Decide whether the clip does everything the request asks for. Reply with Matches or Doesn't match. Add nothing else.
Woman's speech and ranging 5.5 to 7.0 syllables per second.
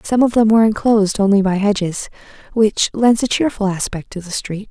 Matches